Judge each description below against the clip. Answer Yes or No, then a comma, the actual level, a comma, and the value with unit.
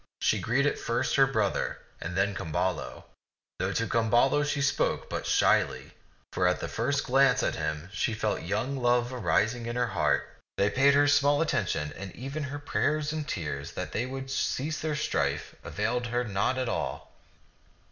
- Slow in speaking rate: No, average, 175 wpm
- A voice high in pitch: No, low, 125 Hz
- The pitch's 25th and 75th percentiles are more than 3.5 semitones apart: Yes, average, 5.3 semitones